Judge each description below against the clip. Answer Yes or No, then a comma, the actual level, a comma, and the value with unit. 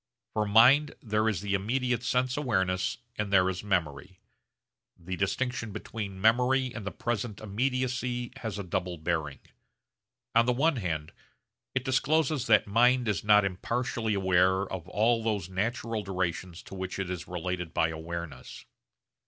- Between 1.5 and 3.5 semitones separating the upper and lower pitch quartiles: No, average, 4.8 semitones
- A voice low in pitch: Yes, low, 105 Hz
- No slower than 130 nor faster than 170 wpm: Yes, average, 150 wpm